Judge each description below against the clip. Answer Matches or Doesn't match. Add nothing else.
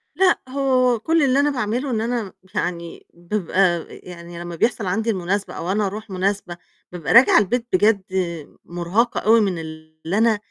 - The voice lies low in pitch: Doesn't match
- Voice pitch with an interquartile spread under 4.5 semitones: Doesn't match